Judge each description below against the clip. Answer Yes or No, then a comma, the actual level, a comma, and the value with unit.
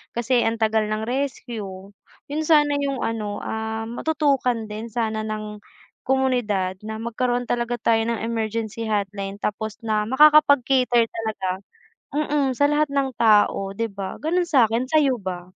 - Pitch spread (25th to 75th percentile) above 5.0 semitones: No, average, 3.7 semitones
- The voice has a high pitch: Yes, high, 230 Hz